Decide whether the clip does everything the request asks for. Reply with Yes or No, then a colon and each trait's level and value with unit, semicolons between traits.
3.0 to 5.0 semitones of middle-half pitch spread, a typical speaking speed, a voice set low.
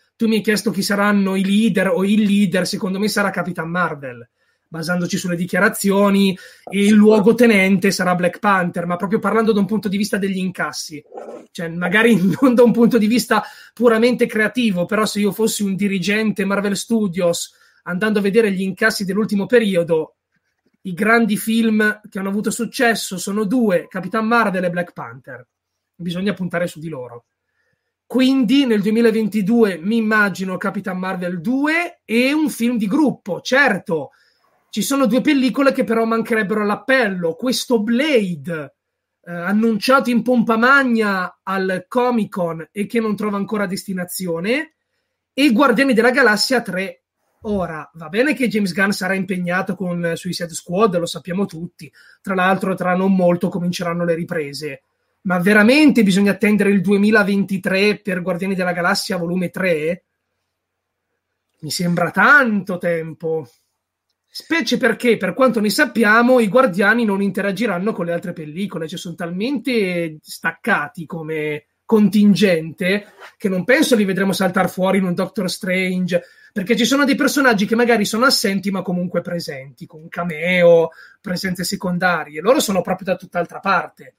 No: average, 4.1 semitones; average, 150 wpm; high, 200 Hz